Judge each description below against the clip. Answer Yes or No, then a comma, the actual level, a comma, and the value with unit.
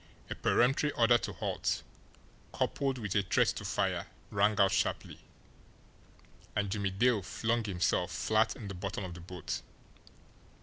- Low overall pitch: Yes, low, 105 Hz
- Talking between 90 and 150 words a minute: Yes, average, 145 wpm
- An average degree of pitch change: Yes, average, 3.3 semitones